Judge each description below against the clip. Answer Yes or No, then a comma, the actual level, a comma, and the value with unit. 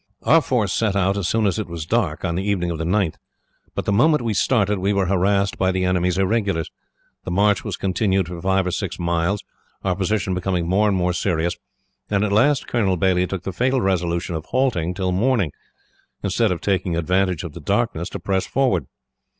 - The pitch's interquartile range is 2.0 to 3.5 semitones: Yes, average, 2.7 semitones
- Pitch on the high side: No, very low, 95 Hz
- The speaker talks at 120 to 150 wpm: No, fast, 205 wpm